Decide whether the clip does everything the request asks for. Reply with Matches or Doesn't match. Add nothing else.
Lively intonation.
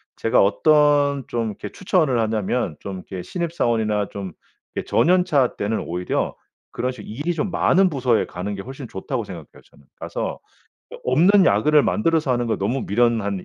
Matches